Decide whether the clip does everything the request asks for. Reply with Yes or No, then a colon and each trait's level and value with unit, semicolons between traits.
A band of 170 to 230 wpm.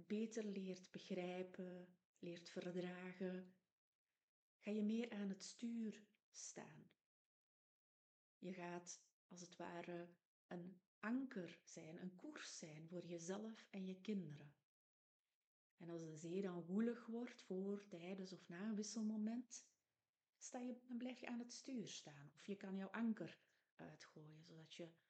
No: average, 140 wpm